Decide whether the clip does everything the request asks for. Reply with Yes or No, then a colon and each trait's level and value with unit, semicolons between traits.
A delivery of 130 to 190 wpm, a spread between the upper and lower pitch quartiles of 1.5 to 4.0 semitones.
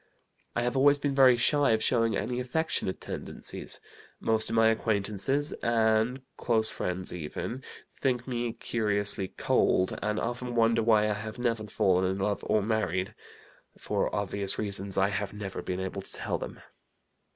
Yes: average, 160 wpm; average, 3.3 semitones